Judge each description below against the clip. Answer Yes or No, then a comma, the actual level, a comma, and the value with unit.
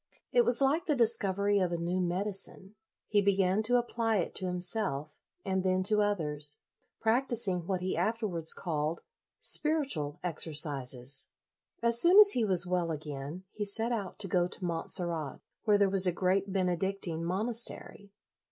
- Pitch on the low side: No, high, 190 Hz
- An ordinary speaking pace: Yes, average, 160 wpm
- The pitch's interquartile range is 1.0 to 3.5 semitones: No, average, 4.3 semitones